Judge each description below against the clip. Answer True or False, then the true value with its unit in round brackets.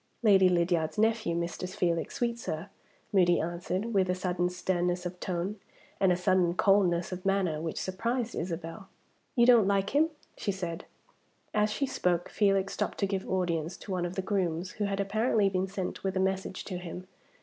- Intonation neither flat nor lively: False (2.2 semitones)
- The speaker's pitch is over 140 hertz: True (185 Hz)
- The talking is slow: False (180 wpm)